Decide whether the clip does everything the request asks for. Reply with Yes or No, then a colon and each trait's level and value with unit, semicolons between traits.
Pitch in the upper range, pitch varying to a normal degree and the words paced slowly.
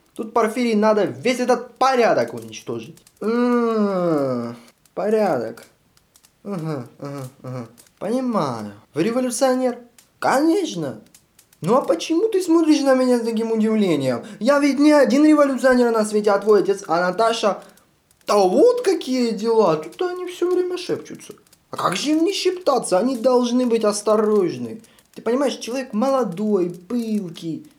No: high, 230 Hz; average, 4.9 semitones; average, 135 wpm